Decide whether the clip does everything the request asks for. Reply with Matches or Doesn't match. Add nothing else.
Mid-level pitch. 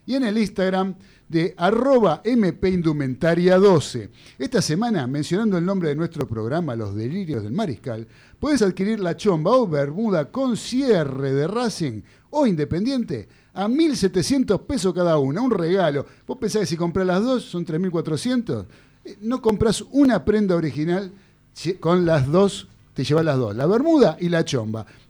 Matches